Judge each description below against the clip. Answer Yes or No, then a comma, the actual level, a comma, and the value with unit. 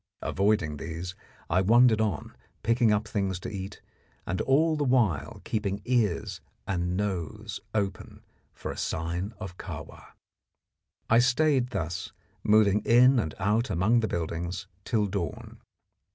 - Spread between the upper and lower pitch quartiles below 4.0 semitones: No, average, 4.4 semitones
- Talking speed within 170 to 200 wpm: No, slow, 135 wpm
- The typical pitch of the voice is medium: No, low, 105 Hz